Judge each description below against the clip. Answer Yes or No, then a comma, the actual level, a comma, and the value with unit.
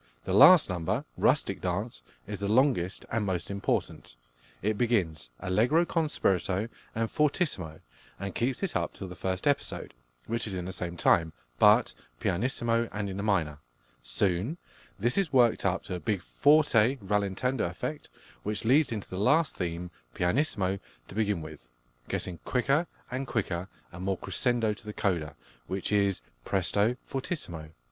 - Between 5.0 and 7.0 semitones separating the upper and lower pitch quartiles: Yes, average, 5.3 semitones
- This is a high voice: No, low, 100 Hz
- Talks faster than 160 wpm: No, average, 155 wpm